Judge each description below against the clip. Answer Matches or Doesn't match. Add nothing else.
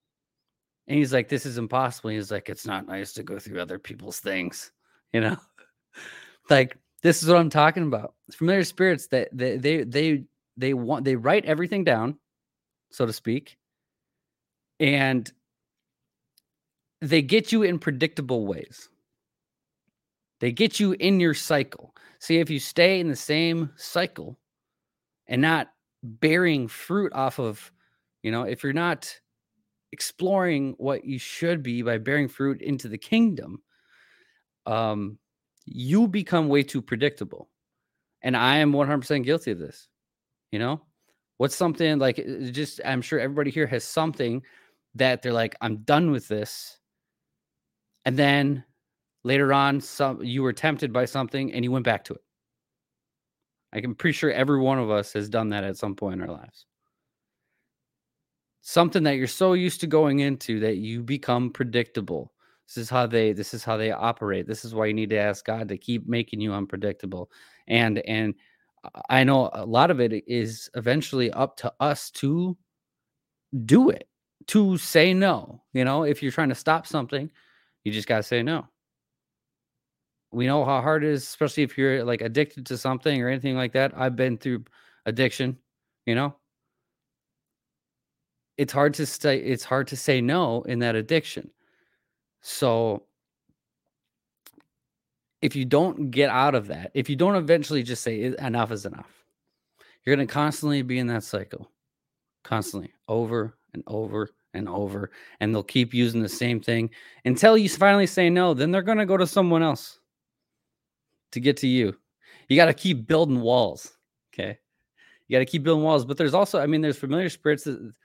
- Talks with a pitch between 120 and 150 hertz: Matches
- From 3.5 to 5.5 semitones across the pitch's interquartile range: Matches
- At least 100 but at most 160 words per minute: Doesn't match